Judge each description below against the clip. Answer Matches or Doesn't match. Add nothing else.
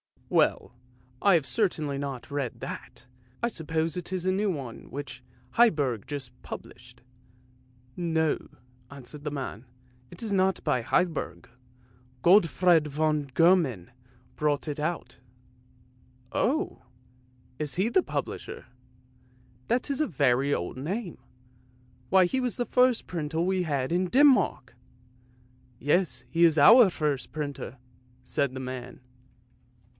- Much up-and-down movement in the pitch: Matches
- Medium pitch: Matches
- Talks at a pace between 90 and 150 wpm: Matches